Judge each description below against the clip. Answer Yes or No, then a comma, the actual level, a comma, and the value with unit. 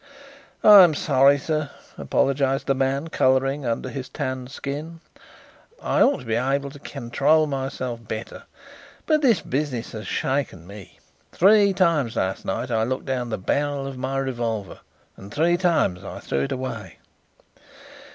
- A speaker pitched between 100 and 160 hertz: Yes, low, 135 Hz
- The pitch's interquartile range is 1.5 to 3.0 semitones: No, average, 3.7 semitones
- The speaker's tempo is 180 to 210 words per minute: No, average, 150 wpm